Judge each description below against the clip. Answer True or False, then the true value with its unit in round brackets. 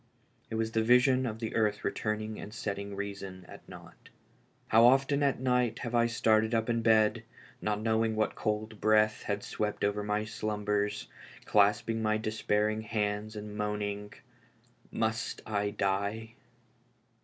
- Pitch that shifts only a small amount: True (1.4 semitones)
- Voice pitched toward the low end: True (110 Hz)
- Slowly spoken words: False (150 wpm)